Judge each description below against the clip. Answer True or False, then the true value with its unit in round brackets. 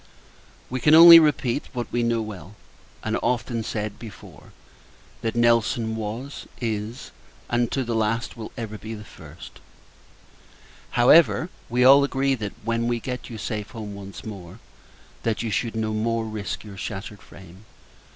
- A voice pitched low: True (115 Hz)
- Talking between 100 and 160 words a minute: True (155 wpm)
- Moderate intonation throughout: False (2.2 semitones)